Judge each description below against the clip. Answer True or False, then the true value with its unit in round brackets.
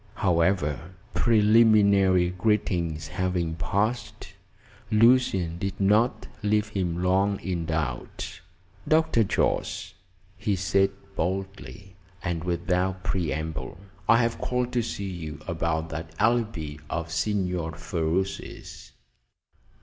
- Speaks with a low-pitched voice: True (95 Hz)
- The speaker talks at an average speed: False (100 wpm)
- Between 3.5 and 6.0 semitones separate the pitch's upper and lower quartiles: True (4.0 semitones)